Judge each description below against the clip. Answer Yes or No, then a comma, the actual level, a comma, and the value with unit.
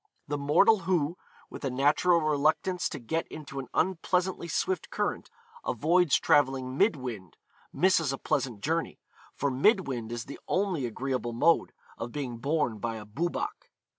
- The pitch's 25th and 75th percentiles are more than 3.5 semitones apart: Yes, average, 5.0 semitones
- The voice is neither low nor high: Yes, medium, 145 Hz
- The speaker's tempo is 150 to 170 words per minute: Yes, average, 155 wpm